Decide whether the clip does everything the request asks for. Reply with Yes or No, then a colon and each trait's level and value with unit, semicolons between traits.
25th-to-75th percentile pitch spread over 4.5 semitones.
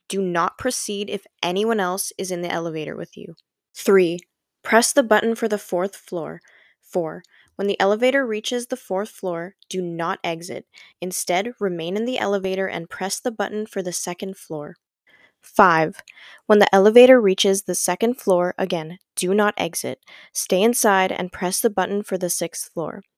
No: average, 2.9 semitones